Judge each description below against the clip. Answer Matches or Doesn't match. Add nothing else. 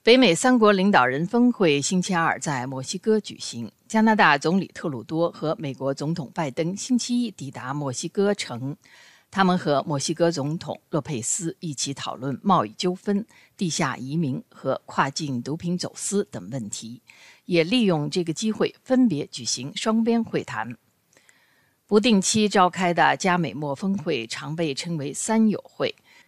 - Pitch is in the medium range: Matches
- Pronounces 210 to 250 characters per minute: Matches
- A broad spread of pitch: Matches